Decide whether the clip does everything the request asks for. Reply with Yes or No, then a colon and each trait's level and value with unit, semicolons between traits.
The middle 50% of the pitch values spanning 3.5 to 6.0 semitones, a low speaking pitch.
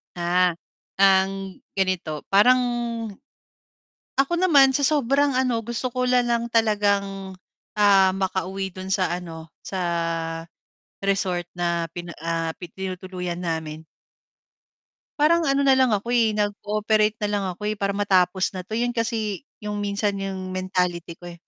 No: average, 3.9 semitones; high, 195 Hz